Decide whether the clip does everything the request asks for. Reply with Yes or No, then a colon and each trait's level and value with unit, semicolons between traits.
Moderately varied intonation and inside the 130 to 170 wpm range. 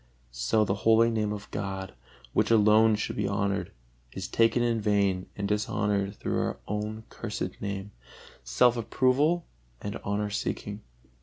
No: narrow, 2.0 semitones; average, 145 wpm